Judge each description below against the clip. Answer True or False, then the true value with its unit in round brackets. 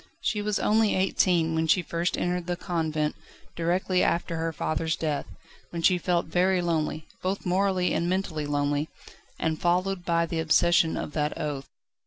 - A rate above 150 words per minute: True (165 wpm)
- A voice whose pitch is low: False (170 Hz)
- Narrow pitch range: True (2.3 semitones)